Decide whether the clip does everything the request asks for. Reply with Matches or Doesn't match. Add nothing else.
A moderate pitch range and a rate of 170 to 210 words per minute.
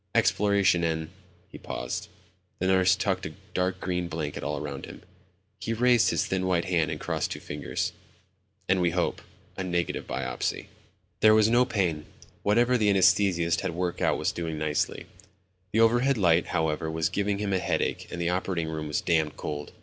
Matches